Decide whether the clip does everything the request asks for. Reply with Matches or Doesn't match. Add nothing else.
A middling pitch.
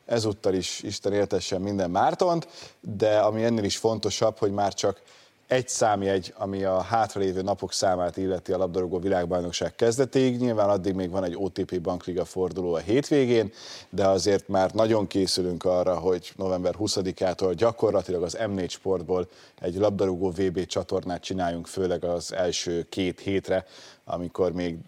Doesn't match